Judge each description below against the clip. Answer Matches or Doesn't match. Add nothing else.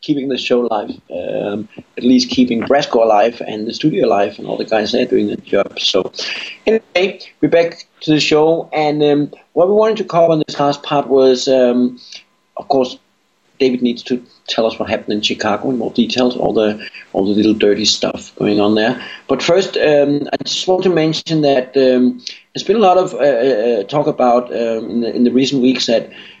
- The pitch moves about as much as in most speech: Matches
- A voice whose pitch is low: Matches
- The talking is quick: Matches